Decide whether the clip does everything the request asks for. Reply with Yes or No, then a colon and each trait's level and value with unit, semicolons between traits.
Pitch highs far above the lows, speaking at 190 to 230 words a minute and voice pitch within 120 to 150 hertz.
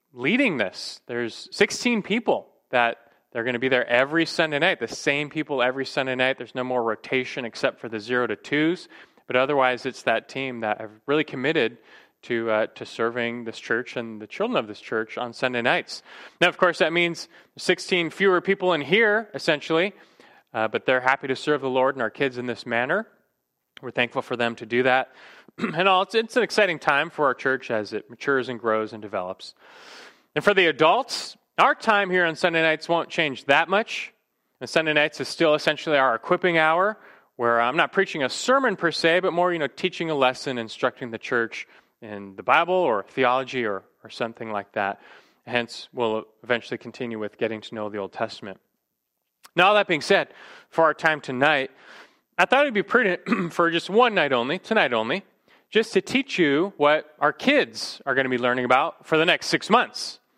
Yes: wide, 6.3 semitones; fast, 205 wpm; low, 135 Hz